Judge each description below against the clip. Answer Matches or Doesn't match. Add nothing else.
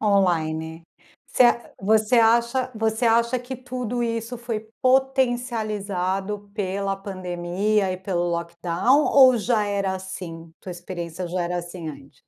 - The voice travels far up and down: Doesn't match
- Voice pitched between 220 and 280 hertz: Doesn't match